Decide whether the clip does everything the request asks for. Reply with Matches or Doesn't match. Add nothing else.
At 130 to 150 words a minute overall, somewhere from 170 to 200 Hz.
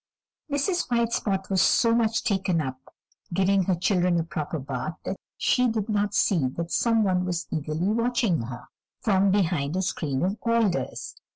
Doesn't match